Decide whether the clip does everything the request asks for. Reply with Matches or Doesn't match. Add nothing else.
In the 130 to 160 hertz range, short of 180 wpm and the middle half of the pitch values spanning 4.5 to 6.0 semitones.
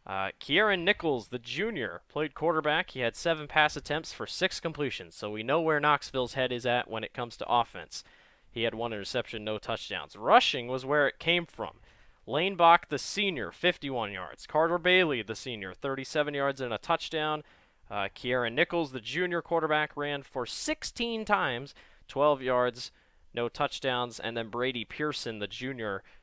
Matches